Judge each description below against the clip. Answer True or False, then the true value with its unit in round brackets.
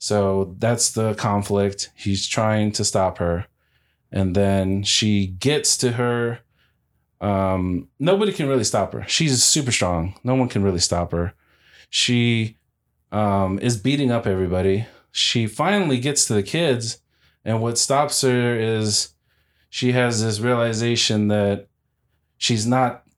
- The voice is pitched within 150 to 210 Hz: False (110 Hz)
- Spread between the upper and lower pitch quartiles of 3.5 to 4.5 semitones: True (3.9 semitones)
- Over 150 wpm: False (140 wpm)